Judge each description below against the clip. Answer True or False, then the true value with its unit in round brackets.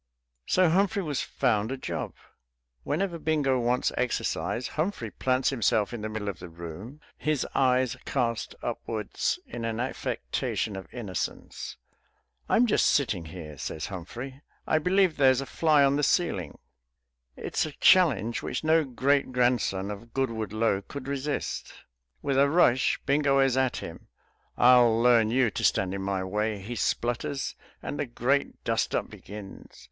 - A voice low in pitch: True (125 Hz)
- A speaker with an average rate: True (155 wpm)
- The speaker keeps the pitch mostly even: False (4.6 semitones)